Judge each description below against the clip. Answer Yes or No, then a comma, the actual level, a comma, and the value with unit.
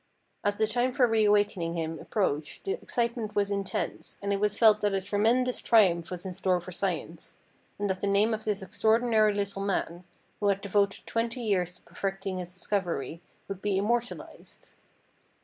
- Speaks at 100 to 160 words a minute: No, average, 180 wpm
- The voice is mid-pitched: No, high, 200 Hz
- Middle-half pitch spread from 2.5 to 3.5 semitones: Yes, average, 2.8 semitones